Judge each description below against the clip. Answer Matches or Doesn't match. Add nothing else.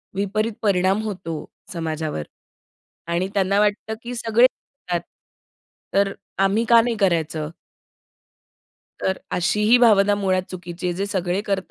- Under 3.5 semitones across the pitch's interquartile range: Matches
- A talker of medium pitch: Doesn't match